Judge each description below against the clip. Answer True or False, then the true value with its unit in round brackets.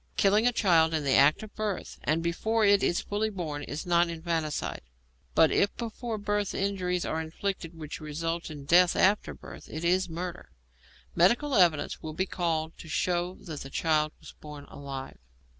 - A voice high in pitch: False (170 Hz)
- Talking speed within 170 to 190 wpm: True (175 wpm)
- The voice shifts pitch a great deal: False (3.9 semitones)